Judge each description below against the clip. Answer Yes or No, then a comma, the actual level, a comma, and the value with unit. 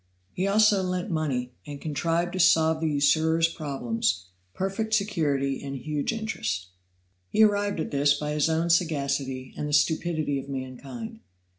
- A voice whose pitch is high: No, medium, 155 Hz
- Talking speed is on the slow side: No, average, 150 wpm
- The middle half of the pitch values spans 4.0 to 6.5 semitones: Yes, average, 4.6 semitones